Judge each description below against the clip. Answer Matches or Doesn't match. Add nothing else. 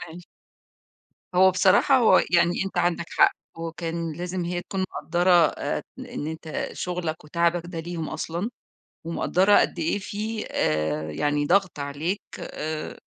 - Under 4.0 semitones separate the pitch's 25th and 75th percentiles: Matches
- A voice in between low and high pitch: Matches